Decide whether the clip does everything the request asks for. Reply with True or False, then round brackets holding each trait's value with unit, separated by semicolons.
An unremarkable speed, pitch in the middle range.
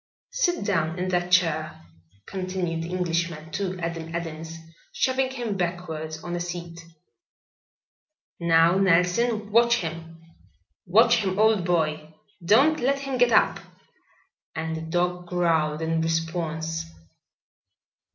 False (120 wpm; 175 Hz)